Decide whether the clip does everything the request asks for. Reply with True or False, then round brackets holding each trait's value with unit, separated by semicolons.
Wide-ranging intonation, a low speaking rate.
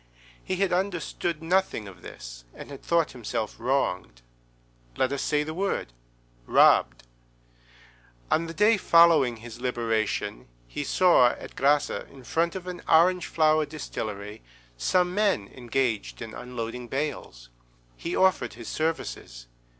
True (7.6 semitones; 130 wpm)